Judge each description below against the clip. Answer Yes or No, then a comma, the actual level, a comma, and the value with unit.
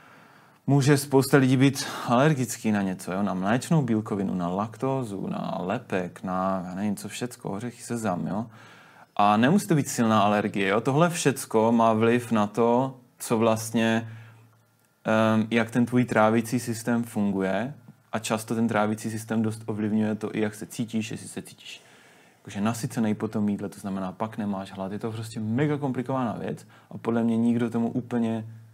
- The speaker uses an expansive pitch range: No, narrow, 2.4 semitones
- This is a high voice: No, low, 115 Hz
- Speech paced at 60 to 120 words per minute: No, fast, 170 wpm